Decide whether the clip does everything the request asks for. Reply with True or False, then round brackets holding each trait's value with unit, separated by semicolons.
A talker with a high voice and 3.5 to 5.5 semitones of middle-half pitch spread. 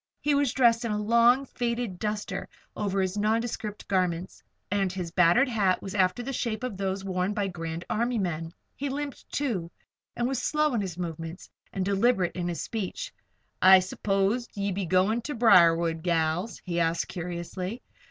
True (195 Hz; 4.7 semitones)